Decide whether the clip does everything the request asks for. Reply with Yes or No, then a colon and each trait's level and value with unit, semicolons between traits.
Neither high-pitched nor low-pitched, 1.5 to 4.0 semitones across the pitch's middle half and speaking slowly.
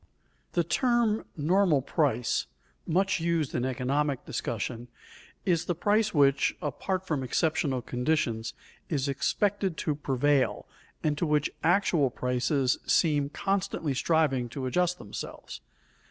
No: medium, 150 Hz; average, 5.2 semitones; slow, 125 wpm